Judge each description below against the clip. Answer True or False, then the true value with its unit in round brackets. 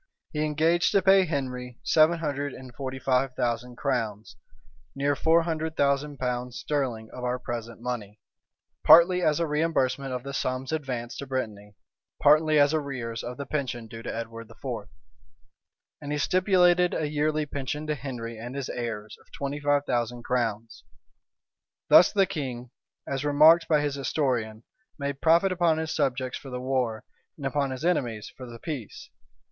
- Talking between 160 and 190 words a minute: True (165 wpm)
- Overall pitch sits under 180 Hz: True (135 Hz)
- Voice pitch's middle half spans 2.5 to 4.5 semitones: True (3.9 semitones)